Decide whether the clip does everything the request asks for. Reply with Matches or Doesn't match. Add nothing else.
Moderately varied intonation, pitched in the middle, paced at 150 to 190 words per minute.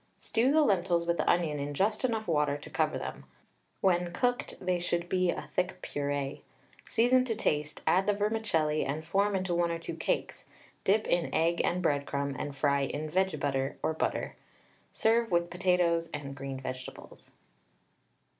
Matches